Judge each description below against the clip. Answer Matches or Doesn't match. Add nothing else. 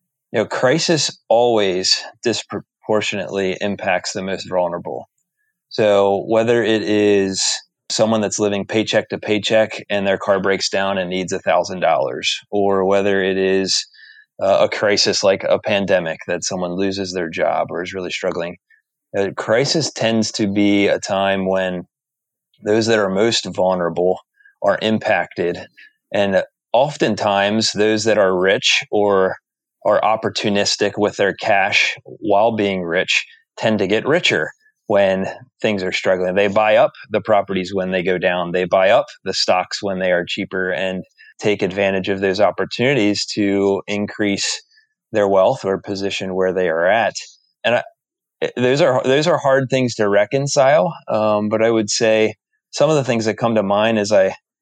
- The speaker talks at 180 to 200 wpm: Doesn't match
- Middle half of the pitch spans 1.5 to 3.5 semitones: Matches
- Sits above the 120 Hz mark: Doesn't match